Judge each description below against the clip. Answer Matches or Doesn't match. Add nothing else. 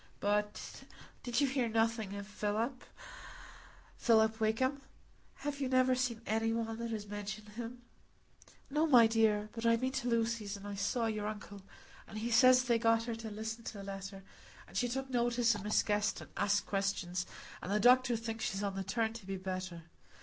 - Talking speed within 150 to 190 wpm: Matches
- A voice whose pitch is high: Matches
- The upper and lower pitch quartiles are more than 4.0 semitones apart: Doesn't match